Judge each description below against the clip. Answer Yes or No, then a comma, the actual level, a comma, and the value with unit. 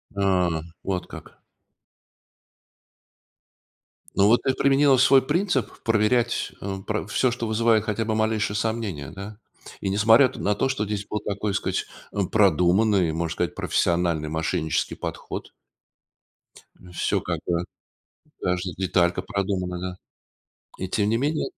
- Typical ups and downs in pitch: Yes, average, 3.8 semitones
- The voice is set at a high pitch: No, low, 105 Hz